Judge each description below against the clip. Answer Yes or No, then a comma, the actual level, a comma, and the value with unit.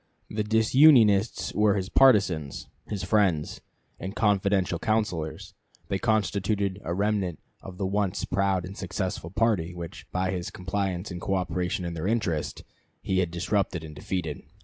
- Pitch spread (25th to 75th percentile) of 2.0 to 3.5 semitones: Yes, average, 2.9 semitones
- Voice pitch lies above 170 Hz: No, very low, 95 Hz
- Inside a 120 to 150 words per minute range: Yes, average, 145 wpm